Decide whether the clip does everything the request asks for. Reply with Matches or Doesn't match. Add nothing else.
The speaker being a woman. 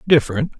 Doesn't match